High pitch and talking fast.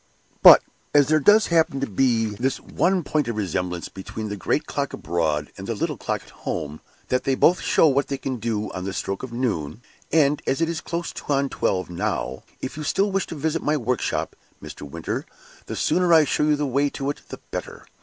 No: low, 135 Hz; fast, 215 wpm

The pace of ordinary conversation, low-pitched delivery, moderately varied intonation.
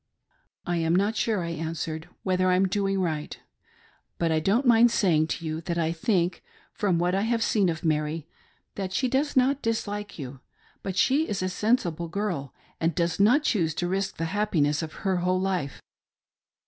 No: average, 190 wpm; medium, 185 Hz; average, 4.1 semitones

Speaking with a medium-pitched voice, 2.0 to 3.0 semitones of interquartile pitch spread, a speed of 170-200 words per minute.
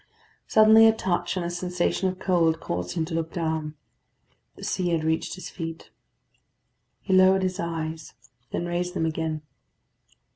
No: medium, 175 Hz; narrow, 2.4 semitones; average, 155 wpm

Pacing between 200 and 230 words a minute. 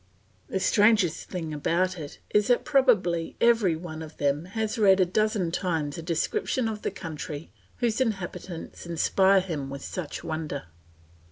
No: average, 155 wpm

